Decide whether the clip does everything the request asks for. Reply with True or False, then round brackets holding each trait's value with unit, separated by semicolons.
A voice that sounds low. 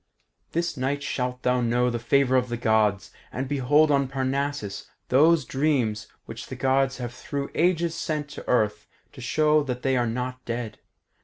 True (130 Hz)